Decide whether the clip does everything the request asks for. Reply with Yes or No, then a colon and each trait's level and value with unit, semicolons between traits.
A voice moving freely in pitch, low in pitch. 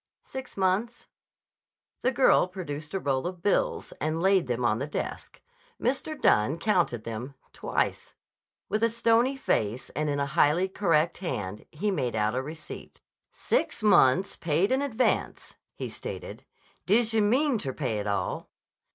No: wide, 8.4 semitones; medium, 170 Hz